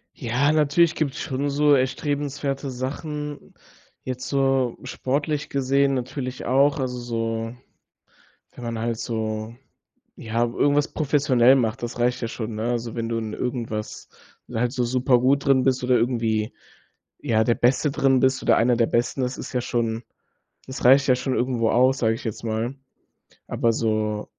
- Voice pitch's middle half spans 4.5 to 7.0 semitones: No, average, 2.8 semitones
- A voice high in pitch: No, low, 125 Hz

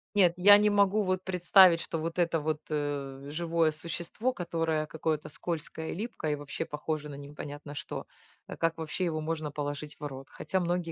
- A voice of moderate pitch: Yes, medium, 160 Hz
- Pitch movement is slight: No, average, 3.0 semitones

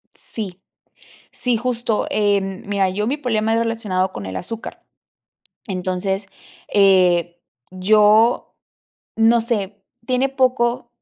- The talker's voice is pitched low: No, high, 210 Hz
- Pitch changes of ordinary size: Yes, average, 3.5 semitones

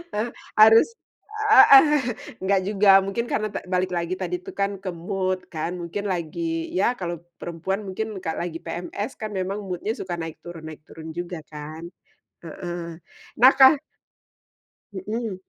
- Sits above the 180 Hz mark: Yes, high, 190 Hz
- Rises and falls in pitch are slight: No, average, 3.9 semitones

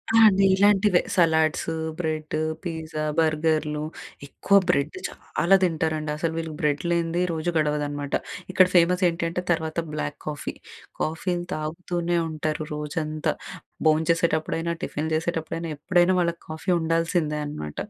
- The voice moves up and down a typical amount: No, narrow, 1.9 semitones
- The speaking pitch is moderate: Yes, medium, 160 Hz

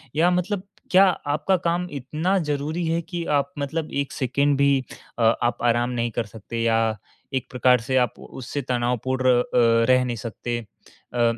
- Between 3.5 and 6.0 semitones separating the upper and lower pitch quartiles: Yes, average, 4.4 semitones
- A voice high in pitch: No, low, 130 Hz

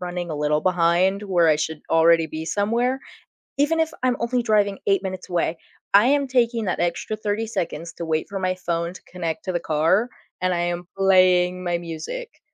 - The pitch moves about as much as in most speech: Yes, average, 3.9 semitones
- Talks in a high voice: No, medium, 180 Hz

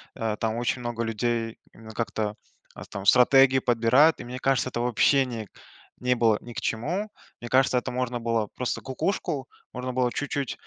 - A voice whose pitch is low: Yes, low, 120 Hz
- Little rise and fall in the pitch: Yes, narrow, 2.3 semitones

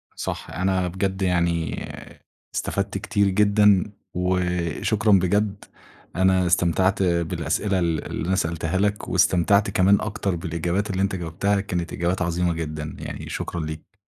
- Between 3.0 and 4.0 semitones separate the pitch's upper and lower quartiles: No, narrow, 2.5 semitones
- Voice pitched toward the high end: No, very low, 90 Hz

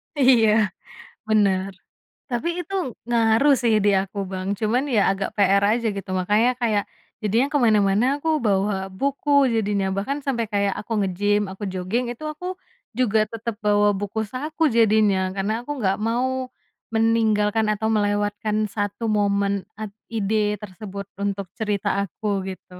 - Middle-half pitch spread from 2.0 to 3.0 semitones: Yes, narrow, 2.4 semitones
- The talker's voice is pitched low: No, high, 210 Hz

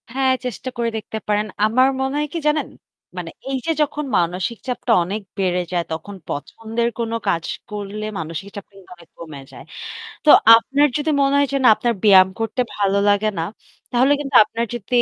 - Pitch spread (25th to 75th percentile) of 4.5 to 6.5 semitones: Yes, average, 5.0 semitones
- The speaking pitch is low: No, high, 220 Hz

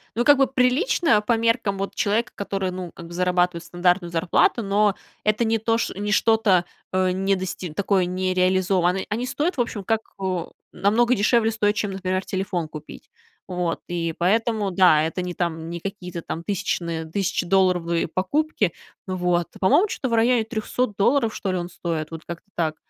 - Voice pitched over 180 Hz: Yes, high, 190 Hz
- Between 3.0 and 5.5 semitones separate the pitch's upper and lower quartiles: Yes, average, 3.9 semitones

